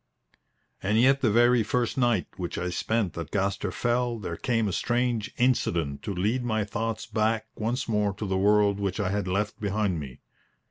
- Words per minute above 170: Yes, average, 185 wpm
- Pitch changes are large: No, average, 3.4 semitones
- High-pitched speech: No, low, 105 Hz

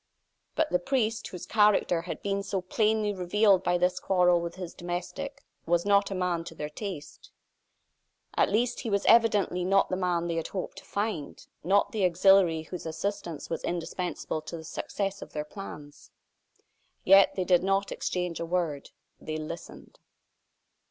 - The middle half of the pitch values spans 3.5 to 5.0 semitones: No, average, 2.8 semitones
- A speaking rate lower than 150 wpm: No, average, 165 wpm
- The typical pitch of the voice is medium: Yes, medium, 180 Hz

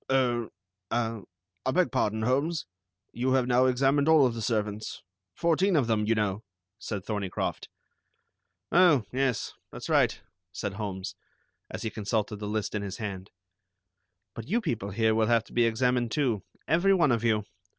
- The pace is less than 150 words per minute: No, average, 165 wpm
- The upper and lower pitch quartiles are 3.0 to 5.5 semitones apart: Yes, average, 3.9 semitones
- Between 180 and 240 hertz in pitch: No, low, 115 Hz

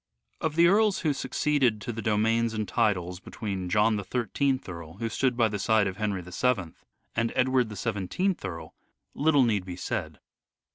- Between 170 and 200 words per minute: Yes, average, 180 wpm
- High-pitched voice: No, low, 110 Hz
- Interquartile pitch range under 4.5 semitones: No, average, 5.0 semitones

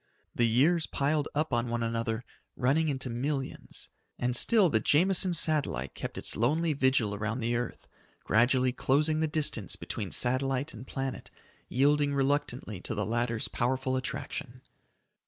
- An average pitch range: Yes, average, 3.9 semitones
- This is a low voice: Yes, low, 130 Hz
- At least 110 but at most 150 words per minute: Yes, average, 145 wpm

